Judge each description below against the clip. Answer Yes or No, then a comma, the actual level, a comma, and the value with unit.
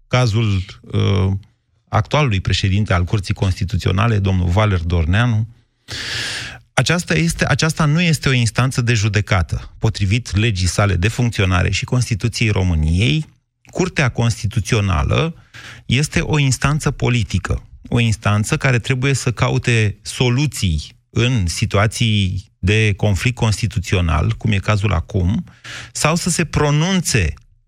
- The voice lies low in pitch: Yes, low, 115 Hz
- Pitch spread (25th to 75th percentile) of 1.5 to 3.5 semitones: No, average, 4.1 semitones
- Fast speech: No, slow, 115 wpm